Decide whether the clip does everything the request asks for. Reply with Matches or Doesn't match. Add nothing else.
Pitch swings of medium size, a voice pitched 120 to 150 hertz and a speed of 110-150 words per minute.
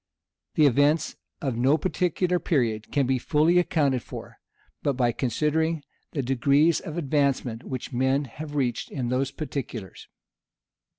Matches